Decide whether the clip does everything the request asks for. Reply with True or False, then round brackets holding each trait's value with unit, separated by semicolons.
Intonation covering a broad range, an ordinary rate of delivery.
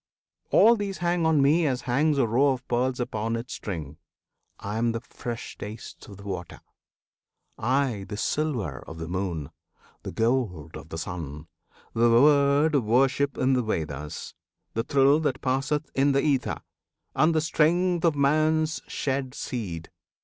True (5.9 semitones; 160 wpm)